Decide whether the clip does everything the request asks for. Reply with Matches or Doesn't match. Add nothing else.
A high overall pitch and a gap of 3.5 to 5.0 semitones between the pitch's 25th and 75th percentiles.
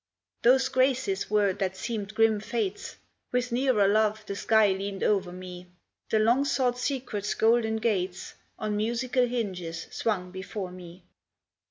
Matches